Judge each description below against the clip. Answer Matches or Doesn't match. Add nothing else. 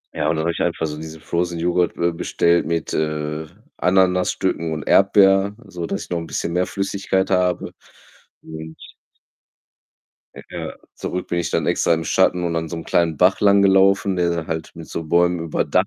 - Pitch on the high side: Doesn't match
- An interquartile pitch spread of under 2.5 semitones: Matches